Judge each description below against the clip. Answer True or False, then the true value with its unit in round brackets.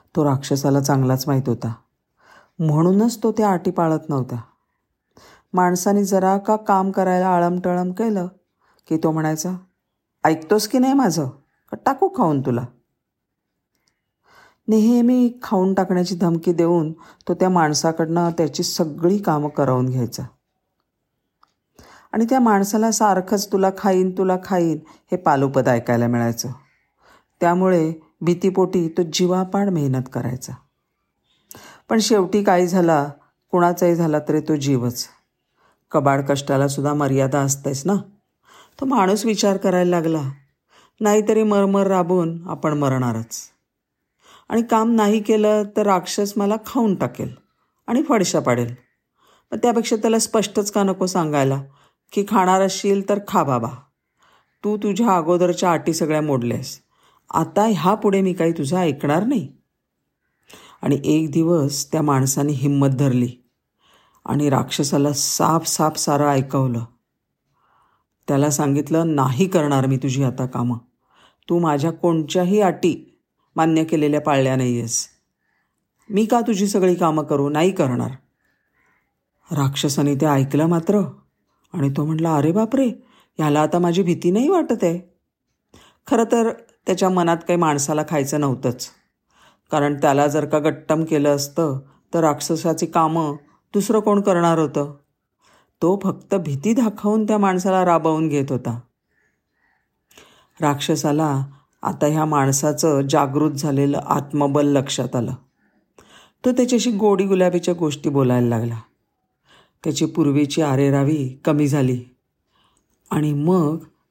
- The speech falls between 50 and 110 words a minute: False (120 wpm)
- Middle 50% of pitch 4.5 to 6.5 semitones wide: True (5.2 semitones)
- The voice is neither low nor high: True (165 Hz)